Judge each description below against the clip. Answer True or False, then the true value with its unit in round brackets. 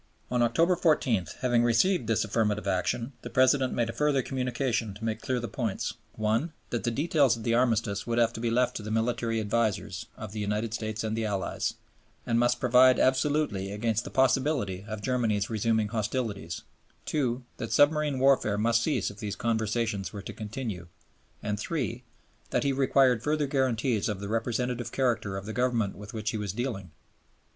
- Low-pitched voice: True (115 Hz)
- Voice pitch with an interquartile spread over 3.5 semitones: False (3.1 semitones)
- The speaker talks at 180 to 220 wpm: True (185 wpm)